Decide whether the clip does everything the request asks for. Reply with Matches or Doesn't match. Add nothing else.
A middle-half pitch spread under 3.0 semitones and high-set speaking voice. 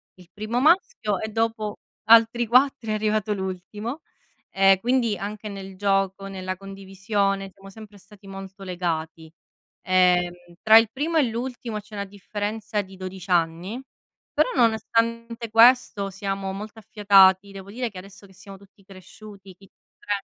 Matches